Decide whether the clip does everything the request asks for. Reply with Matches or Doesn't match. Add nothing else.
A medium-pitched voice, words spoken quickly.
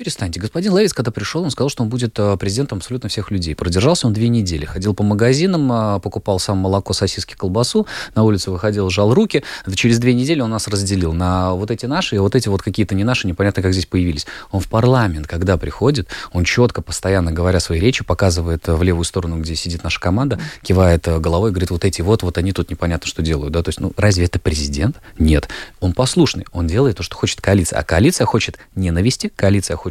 Doesn't match